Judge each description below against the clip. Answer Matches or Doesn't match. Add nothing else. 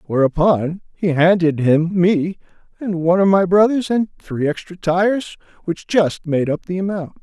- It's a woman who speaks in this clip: Doesn't match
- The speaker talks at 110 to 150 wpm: Doesn't match